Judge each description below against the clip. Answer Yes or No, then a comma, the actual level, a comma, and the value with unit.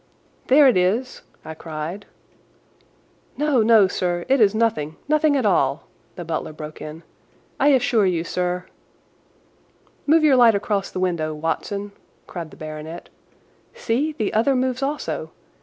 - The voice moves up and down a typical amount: No, wide, 7.6 semitones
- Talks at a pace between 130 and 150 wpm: Yes, average, 140 wpm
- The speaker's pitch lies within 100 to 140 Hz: No, high, 200 Hz